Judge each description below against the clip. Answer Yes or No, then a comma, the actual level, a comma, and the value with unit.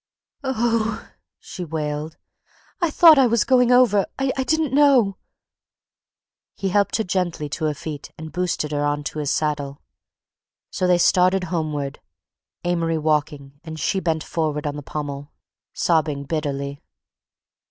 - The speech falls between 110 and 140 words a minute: Yes, slow, 135 wpm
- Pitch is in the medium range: Yes, medium, 160 Hz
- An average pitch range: No, wide, 5.7 semitones